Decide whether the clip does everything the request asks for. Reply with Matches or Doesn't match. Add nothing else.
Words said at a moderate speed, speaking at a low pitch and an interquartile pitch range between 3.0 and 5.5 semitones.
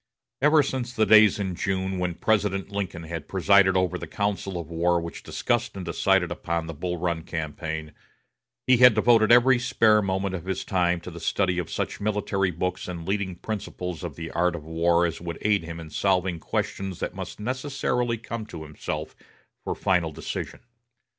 Matches